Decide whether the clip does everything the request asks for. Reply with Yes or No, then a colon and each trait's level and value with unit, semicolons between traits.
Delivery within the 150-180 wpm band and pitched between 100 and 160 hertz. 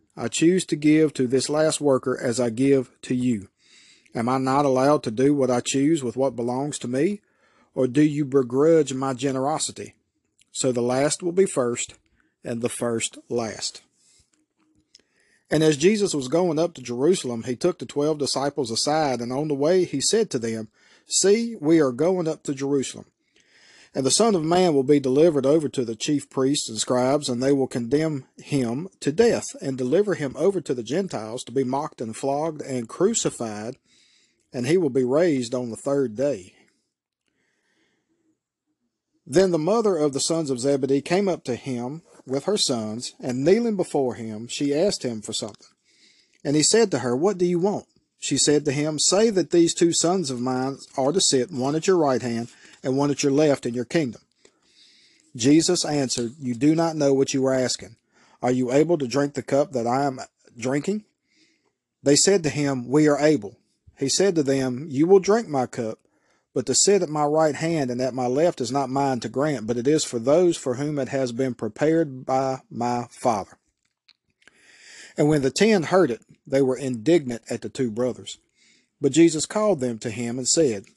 No: average, 195 wpm; medium, 140 Hz